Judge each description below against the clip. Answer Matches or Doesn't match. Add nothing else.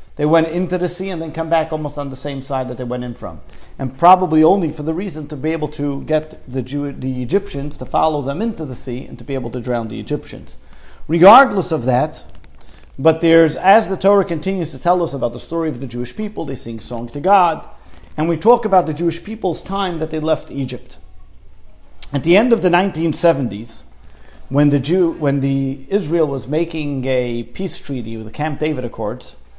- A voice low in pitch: Doesn't match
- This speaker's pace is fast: Matches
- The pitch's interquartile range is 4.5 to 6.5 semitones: Matches